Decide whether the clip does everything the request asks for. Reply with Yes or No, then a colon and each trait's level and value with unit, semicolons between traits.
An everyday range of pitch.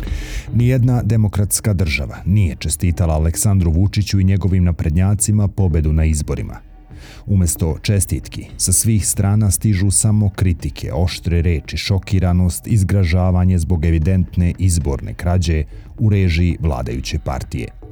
Yes: average, 3.7 semitones